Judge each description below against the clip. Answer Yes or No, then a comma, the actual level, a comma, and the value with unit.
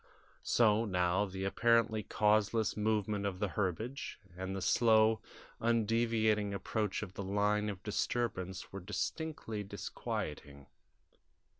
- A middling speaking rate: No, slow, 115 wpm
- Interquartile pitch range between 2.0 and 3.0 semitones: Yes, narrow, 2.5 semitones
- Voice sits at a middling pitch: No, low, 105 Hz